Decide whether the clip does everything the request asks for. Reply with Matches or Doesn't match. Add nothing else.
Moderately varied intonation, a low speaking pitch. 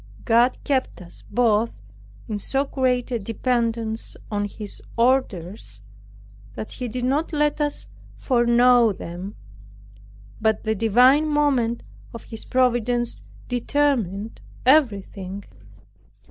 Doesn't match